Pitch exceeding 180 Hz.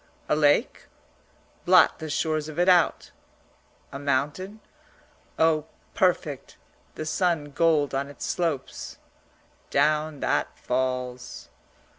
No: medium, 150 Hz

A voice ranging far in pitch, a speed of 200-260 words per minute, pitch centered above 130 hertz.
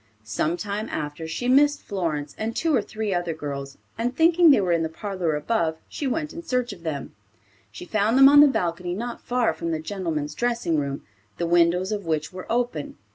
Yes: wide, 7.0 semitones; fast, 205 wpm; medium, 185 Hz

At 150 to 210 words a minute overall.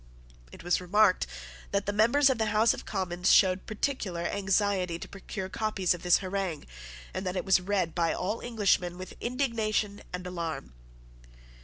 Yes: average, 165 wpm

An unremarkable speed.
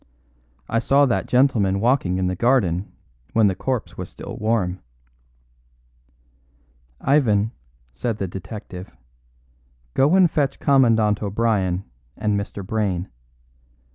No: slow, 110 wpm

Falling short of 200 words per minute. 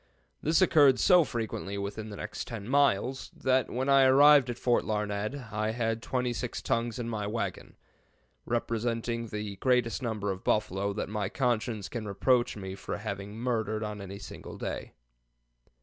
Yes: average, 165 wpm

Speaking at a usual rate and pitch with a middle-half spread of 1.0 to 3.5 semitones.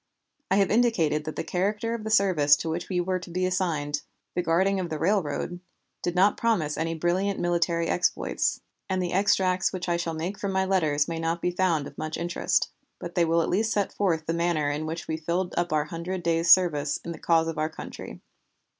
No: fast, 220 wpm; narrow, 2.6 semitones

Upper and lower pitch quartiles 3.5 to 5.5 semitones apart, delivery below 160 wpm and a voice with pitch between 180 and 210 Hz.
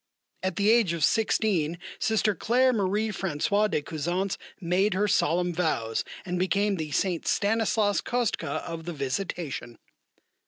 Yes: average, 4.0 semitones; average, 140 wpm; medium, 185 Hz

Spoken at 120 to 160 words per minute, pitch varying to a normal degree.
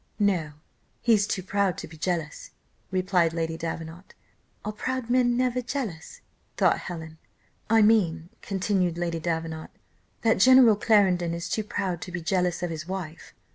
Yes: average, 150 wpm; average, 4.3 semitones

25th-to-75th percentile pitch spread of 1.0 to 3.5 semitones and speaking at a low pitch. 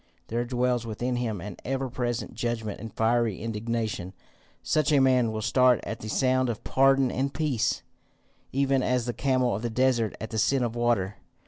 Yes: narrow, 2.5 semitones; low, 120 Hz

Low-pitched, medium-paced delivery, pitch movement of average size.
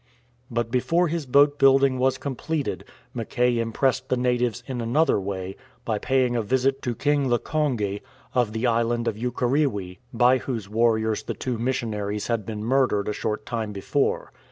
Yes: low, 120 Hz; average, 160 wpm; average, 3.1 semitones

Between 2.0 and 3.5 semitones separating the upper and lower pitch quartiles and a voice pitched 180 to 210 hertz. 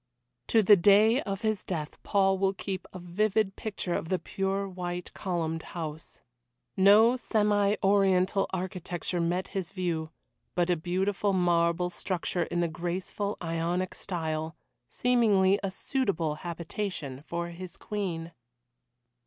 Yes: average, 2.7 semitones; medium, 185 Hz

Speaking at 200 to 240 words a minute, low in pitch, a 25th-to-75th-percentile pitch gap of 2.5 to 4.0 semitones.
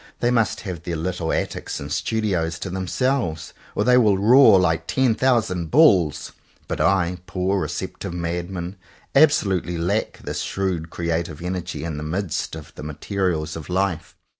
No: average, 160 wpm; very low, 90 Hz; average, 3.4 semitones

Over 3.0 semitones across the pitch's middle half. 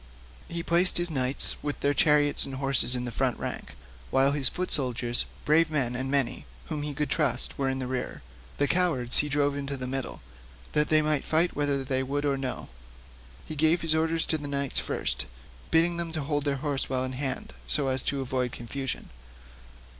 No: narrow, 2.6 semitones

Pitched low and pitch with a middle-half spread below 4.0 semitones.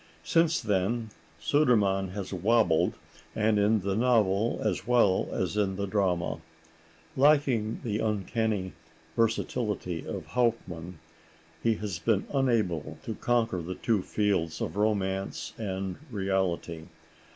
Yes: low, 105 Hz; average, 3.4 semitones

